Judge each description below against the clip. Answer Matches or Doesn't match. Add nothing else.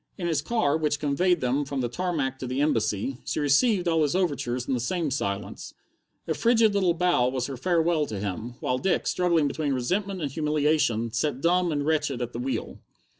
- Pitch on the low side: Doesn't match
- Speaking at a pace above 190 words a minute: Matches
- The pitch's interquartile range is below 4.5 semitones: Doesn't match